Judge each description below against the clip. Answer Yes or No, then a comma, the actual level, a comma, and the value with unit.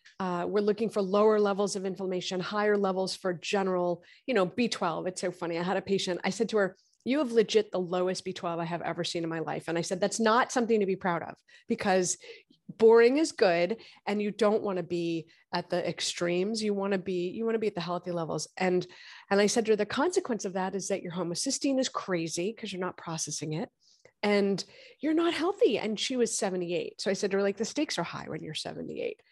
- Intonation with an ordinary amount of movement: Yes, average, 3.8 semitones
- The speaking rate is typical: No, fast, 235 wpm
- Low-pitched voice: No, high, 195 Hz